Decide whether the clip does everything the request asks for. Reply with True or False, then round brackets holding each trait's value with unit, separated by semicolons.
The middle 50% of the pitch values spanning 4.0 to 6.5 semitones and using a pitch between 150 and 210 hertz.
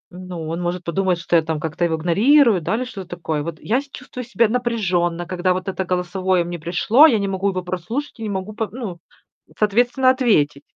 True (4.7 semitones; 185 Hz)